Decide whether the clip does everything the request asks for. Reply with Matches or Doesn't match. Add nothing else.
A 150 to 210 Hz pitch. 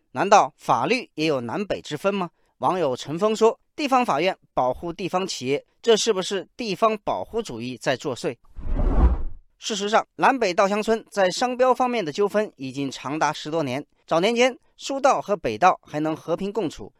Matches